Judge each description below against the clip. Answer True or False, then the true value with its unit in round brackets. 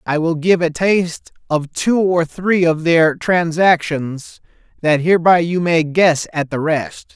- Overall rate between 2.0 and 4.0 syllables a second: True (3.9 syllables/s)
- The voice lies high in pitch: False (165 Hz)